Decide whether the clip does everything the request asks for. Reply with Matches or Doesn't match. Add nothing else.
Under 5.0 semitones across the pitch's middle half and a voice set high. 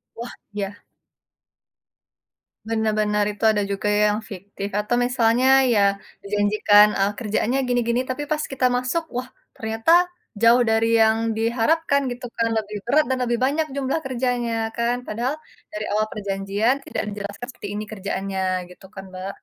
Matches